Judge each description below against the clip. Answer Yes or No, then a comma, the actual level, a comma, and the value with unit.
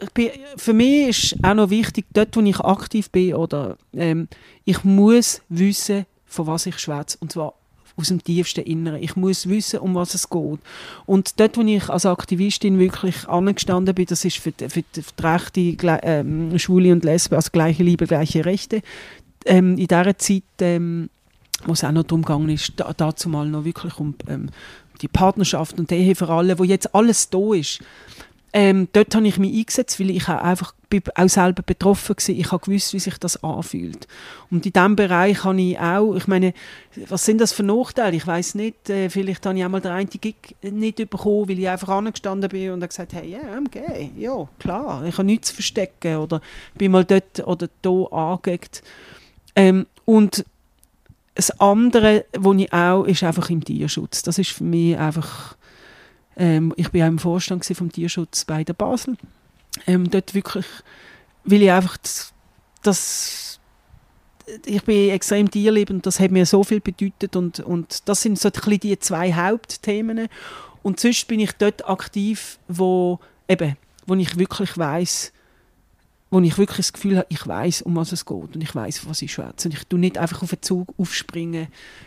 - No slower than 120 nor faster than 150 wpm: No, average, 185 wpm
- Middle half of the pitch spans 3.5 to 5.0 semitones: No, average, 2.7 semitones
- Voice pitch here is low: No, medium, 185 Hz